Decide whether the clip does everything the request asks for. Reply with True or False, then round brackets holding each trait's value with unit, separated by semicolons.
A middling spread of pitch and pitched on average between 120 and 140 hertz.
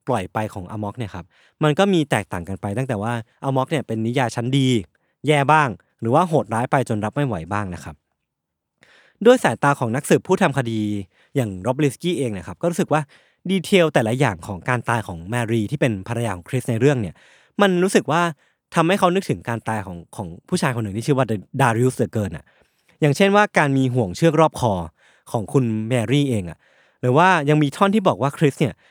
False (5.9 semitones; 130 Hz)